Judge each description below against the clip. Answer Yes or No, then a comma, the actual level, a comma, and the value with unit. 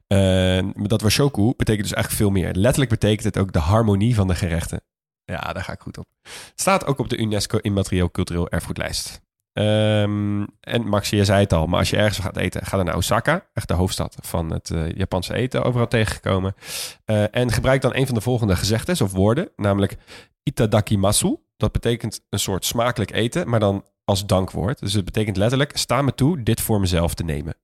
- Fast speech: Yes, fast, 205 wpm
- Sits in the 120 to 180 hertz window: No, low, 105 Hz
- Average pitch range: Yes, average, 3.5 semitones